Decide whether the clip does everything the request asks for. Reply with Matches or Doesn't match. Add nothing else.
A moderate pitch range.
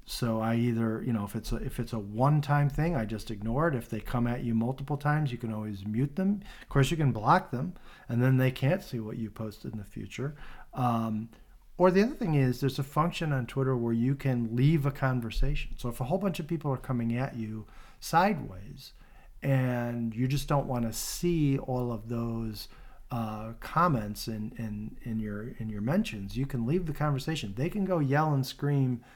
Matches